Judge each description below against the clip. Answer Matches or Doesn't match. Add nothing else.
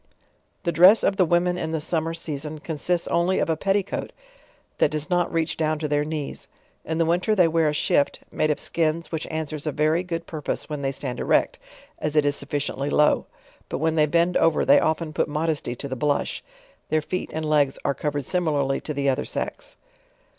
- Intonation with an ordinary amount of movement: Doesn't match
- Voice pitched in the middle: Matches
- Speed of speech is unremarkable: Doesn't match